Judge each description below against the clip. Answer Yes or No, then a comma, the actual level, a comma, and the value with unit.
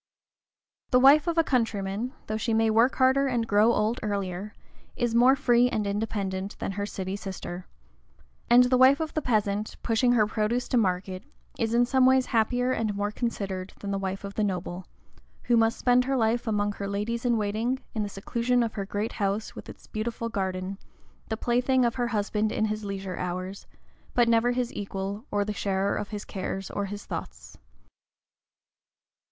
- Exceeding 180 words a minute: Yes, average, 190 wpm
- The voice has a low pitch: No, high, 215 Hz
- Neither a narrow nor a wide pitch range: Yes, average, 3.4 semitones